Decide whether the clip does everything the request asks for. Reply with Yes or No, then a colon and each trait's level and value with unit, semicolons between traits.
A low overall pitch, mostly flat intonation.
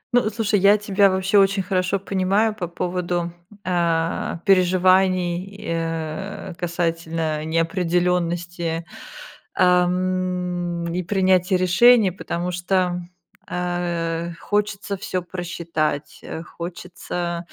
No: medium, 180 Hz; narrow, 1.8 semitones